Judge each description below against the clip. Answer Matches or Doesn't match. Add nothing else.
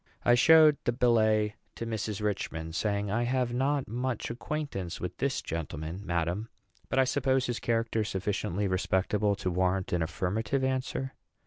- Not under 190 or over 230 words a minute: Doesn't match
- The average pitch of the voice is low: Matches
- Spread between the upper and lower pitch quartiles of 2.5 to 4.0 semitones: Doesn't match